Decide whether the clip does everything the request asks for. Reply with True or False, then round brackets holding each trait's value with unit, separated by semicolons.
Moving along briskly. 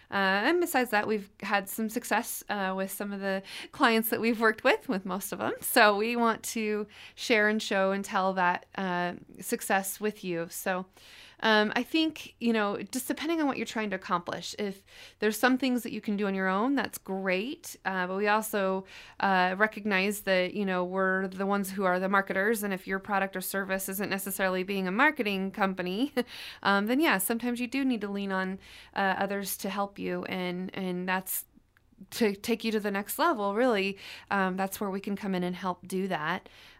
True (210 wpm)